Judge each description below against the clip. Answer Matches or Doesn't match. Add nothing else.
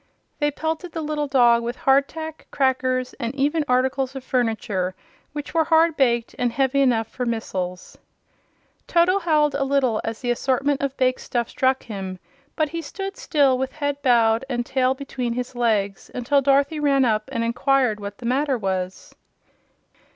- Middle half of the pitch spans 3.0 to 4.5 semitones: Matches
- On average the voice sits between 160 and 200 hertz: Doesn't match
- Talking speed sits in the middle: Matches